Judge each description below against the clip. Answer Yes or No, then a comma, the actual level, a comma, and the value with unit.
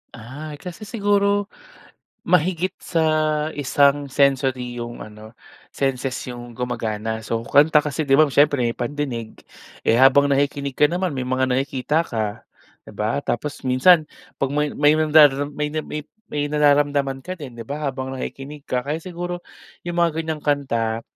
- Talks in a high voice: No, medium, 140 Hz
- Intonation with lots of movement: No, average, 3.2 semitones